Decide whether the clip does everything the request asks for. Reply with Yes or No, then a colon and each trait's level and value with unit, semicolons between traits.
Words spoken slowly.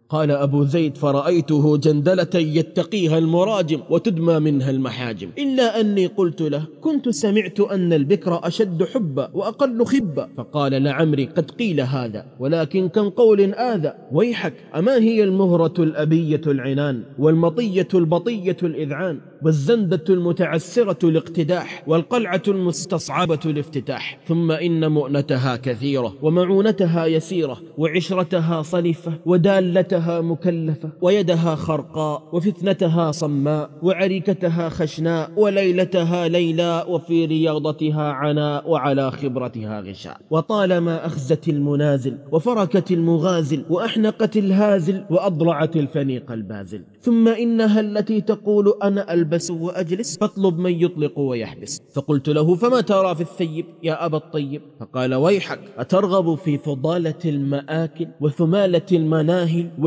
No: average, 110 wpm